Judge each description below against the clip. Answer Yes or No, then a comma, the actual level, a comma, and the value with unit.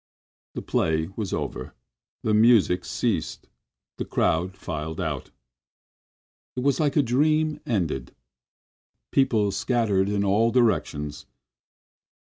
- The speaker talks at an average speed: No, slow, 105 wpm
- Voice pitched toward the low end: Yes, low, 105 Hz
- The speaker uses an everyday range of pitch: No, wide, 6.0 semitones